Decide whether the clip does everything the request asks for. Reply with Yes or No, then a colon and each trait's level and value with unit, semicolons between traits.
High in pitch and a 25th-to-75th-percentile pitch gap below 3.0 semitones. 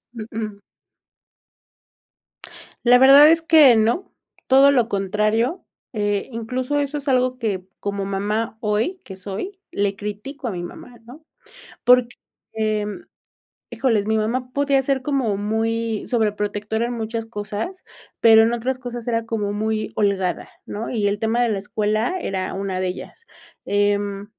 No: high, 225 Hz; average, 3.5 semitones